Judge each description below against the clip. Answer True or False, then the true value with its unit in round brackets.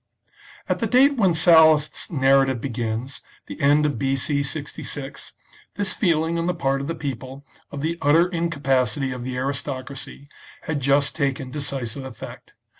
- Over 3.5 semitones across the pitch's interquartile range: False (3.2 semitones)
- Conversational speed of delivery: True (150 wpm)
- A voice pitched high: False (140 Hz)